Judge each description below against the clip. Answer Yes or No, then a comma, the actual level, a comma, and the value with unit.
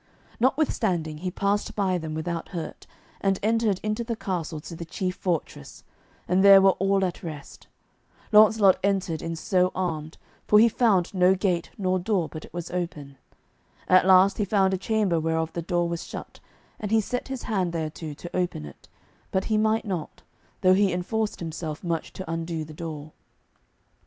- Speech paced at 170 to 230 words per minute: Yes, average, 175 wpm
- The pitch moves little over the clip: No, average, 3.3 semitones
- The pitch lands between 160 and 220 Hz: Yes, medium, 185 Hz